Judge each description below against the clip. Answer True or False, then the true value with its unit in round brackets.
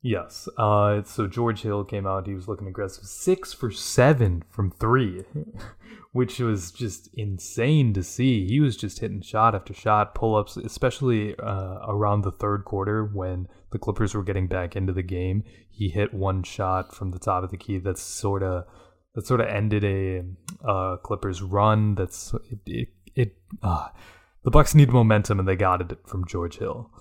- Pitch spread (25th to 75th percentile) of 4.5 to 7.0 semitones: False (3.2 semitones)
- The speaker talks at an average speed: True (180 wpm)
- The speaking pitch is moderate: False (100 Hz)